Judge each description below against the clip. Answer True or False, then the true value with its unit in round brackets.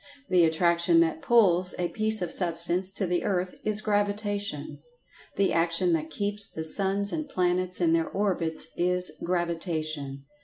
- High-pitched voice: False (180 Hz)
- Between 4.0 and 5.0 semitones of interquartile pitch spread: False (3.2 semitones)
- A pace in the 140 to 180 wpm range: True (150 wpm)